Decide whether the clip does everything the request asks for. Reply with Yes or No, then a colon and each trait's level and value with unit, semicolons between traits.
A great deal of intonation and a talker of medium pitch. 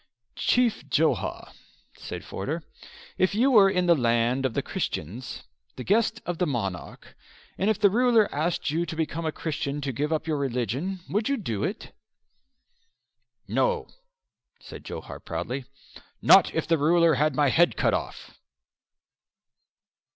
Yes: wide, 6.5 semitones; medium, 160 Hz